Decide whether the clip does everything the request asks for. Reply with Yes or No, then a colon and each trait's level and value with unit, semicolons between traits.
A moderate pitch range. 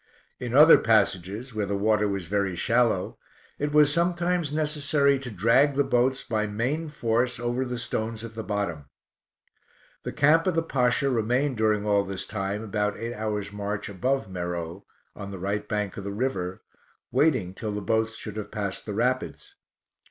Yes: average, 4.5 semitones